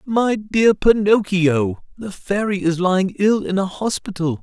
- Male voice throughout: Yes, male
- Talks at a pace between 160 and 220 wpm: No, average, 150 wpm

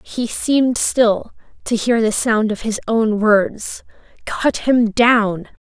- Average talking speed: Yes, average, 150 wpm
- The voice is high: Yes, high, 225 Hz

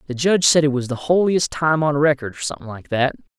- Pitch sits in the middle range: Yes, medium, 145 Hz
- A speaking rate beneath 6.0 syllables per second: No, 6.3 syllables/s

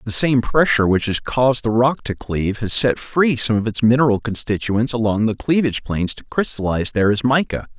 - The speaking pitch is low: Yes, low, 115 Hz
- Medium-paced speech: No, fast, 210 wpm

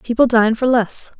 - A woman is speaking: Yes, female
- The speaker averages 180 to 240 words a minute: Yes, average, 200 wpm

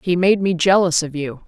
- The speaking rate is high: Yes, fast, 245 wpm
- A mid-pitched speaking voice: Yes, medium, 175 Hz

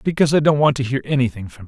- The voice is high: No, low, 135 Hz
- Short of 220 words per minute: No, fast, 320 wpm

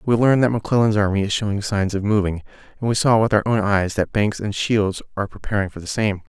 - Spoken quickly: Yes, fast, 245 wpm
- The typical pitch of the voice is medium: No, low, 105 Hz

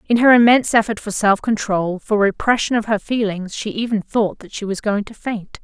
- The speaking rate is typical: No, fast, 225 wpm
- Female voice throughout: Yes, female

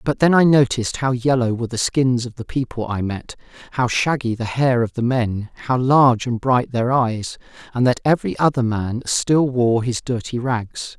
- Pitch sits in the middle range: No, low, 125 Hz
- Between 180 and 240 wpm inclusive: Yes, average, 200 wpm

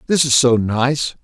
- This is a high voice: No, low, 130 Hz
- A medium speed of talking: Yes, average, 195 wpm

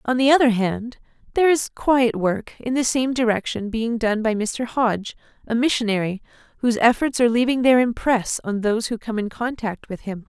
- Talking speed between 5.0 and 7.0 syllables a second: Yes, 5.4 syllables/s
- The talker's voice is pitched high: Yes, high, 235 Hz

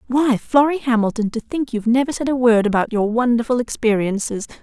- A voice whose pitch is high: Yes, high, 240 Hz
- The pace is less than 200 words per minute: Yes, average, 180 wpm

